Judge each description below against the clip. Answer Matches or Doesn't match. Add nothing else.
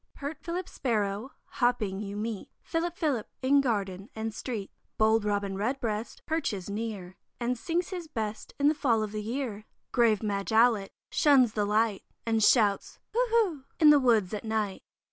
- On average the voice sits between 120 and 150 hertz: Doesn't match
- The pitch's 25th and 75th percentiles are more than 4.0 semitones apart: Matches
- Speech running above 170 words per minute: Doesn't match